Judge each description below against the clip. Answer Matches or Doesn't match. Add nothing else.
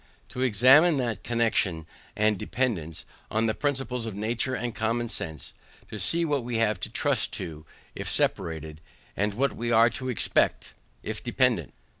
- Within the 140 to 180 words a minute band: Matches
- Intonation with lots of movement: Doesn't match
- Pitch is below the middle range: Matches